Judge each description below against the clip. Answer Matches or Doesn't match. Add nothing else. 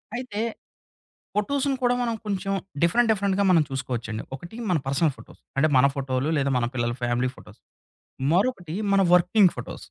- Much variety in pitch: Matches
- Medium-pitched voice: Matches